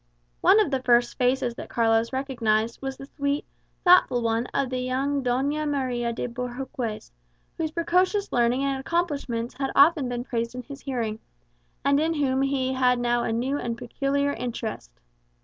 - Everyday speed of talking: Yes, average, 165 wpm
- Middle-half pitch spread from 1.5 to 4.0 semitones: Yes, average, 2.8 semitones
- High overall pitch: Yes, very high, 260 Hz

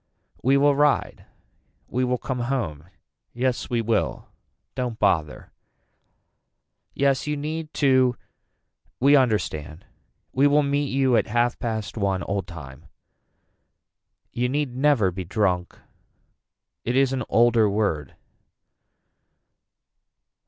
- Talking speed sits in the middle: No, slow, 110 wpm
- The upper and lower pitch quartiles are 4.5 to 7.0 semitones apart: Yes, average, 5.3 semitones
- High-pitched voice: No, low, 120 Hz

